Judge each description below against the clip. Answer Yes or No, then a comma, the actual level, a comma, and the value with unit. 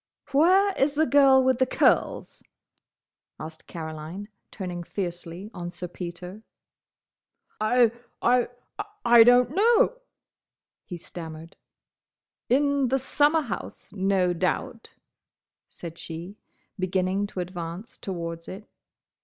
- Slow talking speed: Yes, slow, 95 wpm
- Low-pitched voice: No, high, 200 Hz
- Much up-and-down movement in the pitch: Yes, wide, 7.0 semitones